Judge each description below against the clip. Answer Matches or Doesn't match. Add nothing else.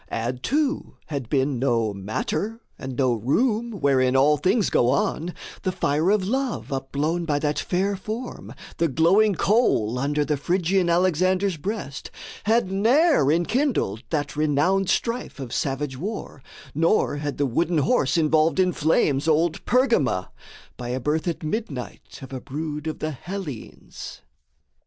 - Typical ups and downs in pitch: Doesn't match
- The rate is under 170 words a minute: Matches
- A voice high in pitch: Doesn't match